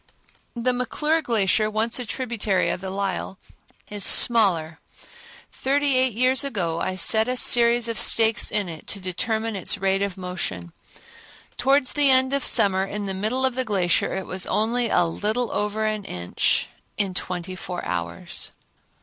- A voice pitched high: Yes, high, 215 Hz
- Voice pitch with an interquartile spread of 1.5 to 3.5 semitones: No, average, 4.6 semitones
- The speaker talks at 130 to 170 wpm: Yes, average, 165 wpm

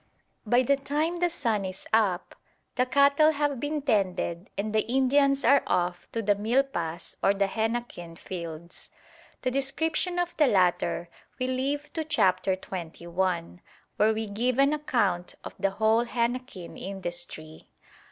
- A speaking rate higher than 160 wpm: No, average, 145 wpm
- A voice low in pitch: No, high, 225 Hz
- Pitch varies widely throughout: Yes, wide, 6.9 semitones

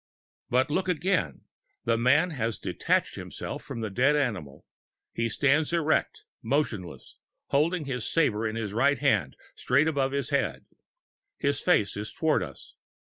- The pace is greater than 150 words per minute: No, average, 145 wpm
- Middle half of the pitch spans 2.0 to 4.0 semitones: No, average, 5.3 semitones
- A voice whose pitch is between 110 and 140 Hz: Yes, low, 135 Hz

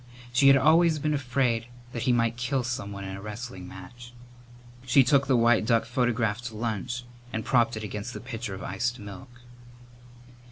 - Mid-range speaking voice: No, low, 120 Hz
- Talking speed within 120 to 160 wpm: No, average, 175 wpm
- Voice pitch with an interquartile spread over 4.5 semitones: No, average, 2.7 semitones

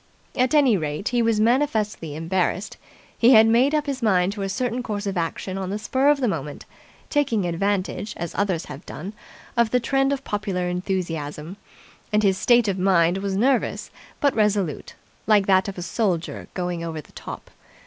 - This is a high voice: Yes, high, 200 Hz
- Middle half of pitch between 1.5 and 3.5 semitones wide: No, average, 4.8 semitones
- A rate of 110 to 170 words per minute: No, average, 185 wpm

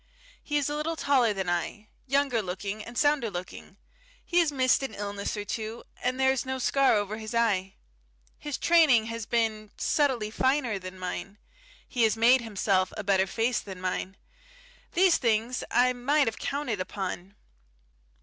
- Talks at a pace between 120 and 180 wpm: Yes, average, 170 wpm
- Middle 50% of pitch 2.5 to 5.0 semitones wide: Yes, average, 4.7 semitones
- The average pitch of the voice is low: No, high, 230 Hz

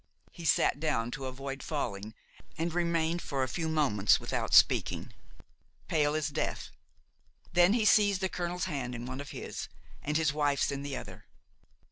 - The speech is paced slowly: No, average, 165 wpm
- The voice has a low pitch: No, medium, 150 Hz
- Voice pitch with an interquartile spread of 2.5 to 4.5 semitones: Yes, average, 4.0 semitones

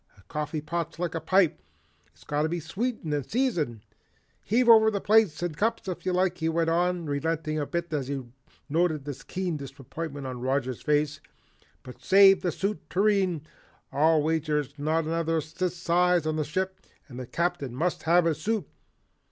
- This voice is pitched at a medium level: Yes, medium, 165 Hz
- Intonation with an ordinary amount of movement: Yes, average, 3.4 semitones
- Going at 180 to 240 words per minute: Yes, average, 185 wpm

